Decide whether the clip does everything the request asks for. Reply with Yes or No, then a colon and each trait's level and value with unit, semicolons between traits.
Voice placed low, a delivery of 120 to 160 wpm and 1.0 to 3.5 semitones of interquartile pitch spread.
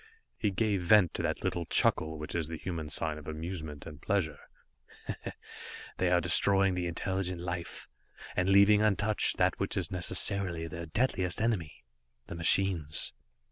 Yes: very low, 90 Hz; average, 150 wpm; average, 3.2 semitones